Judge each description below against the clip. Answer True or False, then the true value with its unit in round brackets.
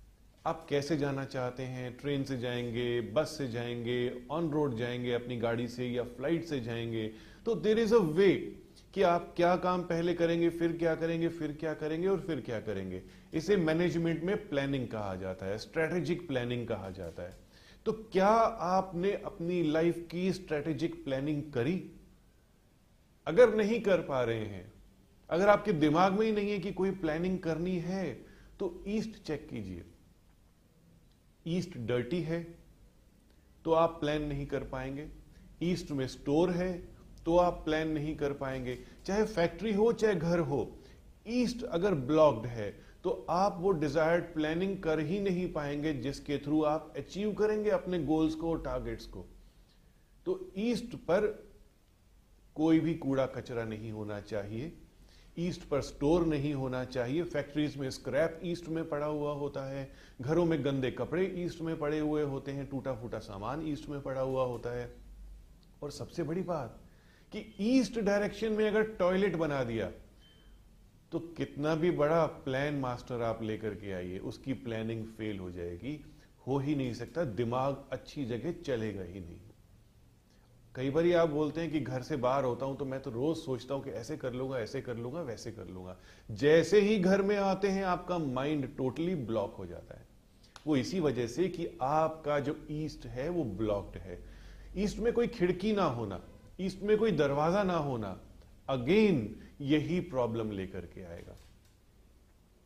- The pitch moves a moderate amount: False (6.1 semitones)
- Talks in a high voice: False (150 Hz)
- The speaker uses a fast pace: False (165 wpm)